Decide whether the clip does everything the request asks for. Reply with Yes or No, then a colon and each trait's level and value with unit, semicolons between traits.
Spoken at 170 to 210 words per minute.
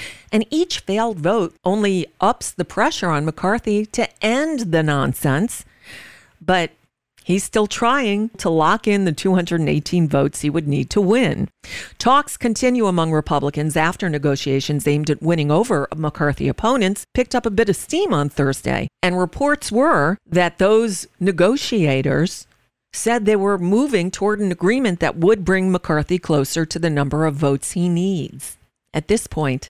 No: average, 155 wpm